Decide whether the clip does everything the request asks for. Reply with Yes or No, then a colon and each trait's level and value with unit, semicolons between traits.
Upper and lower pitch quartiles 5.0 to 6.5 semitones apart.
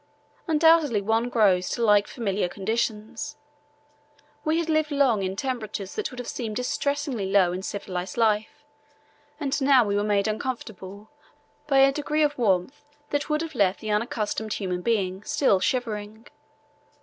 Yes: wide, 5.5 semitones